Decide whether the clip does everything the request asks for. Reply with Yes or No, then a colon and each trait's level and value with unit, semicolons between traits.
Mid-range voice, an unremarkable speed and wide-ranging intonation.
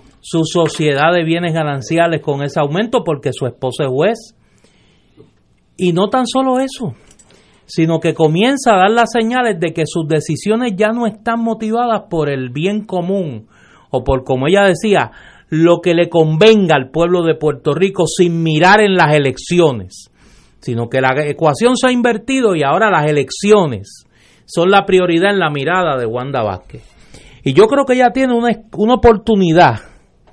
Yes: medium, 175 Hz; average, 170 wpm; wide, 6.3 semitones